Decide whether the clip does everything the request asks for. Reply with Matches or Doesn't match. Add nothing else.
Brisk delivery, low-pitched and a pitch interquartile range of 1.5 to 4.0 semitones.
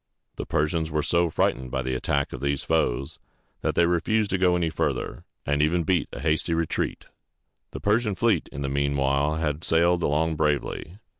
Doesn't match